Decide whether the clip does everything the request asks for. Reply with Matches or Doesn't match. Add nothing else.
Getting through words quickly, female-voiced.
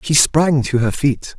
Doesn't match